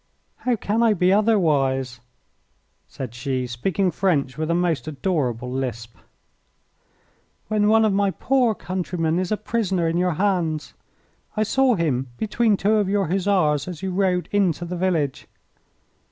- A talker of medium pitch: Yes, medium, 180 Hz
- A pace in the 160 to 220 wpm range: No, average, 150 wpm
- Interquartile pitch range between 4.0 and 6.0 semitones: Yes, wide, 5.4 semitones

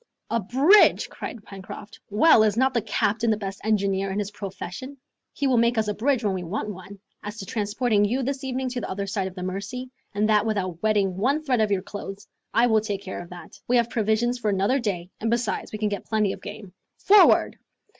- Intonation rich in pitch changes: No, average, 3.3 semitones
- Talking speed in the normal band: No, fast, 225 wpm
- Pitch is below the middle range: No, high, 215 Hz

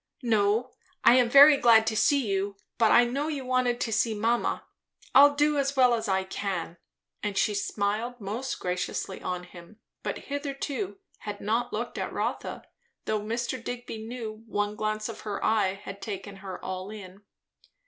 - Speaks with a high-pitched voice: Yes, high, 220 Hz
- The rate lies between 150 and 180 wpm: Yes, average, 170 wpm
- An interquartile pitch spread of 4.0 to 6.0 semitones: No, average, 3.5 semitones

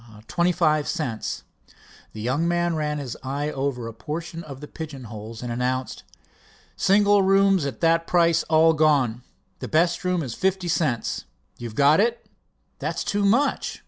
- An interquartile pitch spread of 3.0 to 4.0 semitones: No, average, 5.0 semitones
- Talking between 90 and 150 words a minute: No, average, 165 wpm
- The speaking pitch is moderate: Yes, medium, 155 Hz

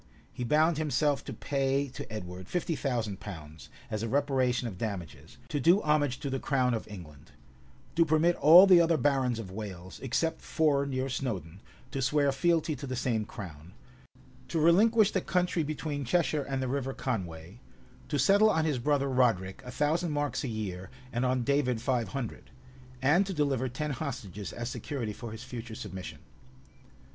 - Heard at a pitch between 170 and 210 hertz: No, low, 130 Hz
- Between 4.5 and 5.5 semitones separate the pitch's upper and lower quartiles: Yes, average, 5.1 semitones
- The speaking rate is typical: Yes, average, 175 wpm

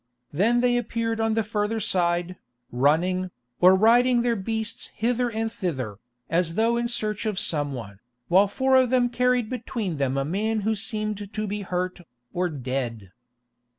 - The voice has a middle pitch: No, high, 210 Hz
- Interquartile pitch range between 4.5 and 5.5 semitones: Yes, average, 4.9 semitones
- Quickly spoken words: No, average, 165 wpm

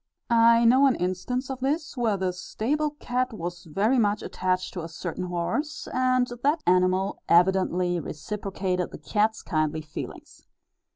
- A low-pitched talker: No, high, 195 Hz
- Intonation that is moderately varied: No, wide, 5.8 semitones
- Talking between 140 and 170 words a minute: Yes, average, 150 wpm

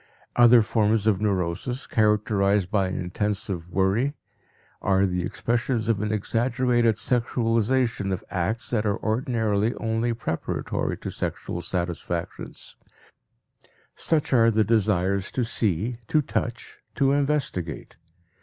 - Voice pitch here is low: Yes, low, 110 Hz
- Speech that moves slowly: Yes, slow, 115 wpm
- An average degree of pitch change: Yes, average, 3.4 semitones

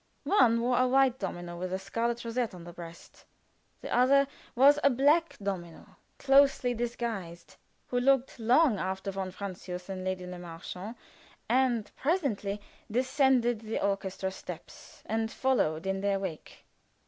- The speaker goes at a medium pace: Yes, average, 145 wpm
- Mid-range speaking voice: No, high, 220 Hz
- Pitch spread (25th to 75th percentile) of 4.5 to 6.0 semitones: Yes, average, 5.3 semitones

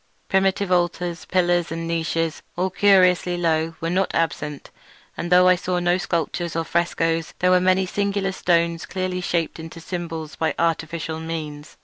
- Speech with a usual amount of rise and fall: No, narrow, 1.8 semitones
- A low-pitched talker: No, medium, 170 Hz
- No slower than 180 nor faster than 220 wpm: No, average, 155 wpm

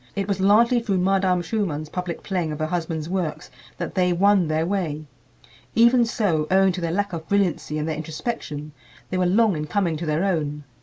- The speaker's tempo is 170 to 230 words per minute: Yes, average, 200 wpm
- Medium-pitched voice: Yes, medium, 180 Hz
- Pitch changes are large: No, average, 4.1 semitones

